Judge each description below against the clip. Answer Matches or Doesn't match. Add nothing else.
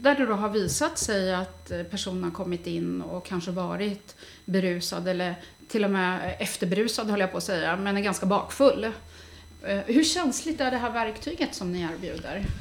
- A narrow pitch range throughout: Doesn't match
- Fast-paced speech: Doesn't match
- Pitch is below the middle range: Doesn't match